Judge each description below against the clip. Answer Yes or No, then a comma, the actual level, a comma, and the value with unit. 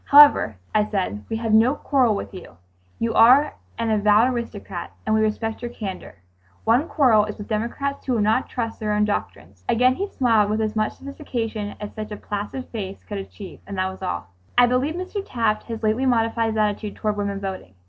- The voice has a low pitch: No, high, 220 Hz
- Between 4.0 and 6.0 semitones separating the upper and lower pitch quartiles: No, average, 2.9 semitones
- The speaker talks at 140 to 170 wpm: No, fast, 205 wpm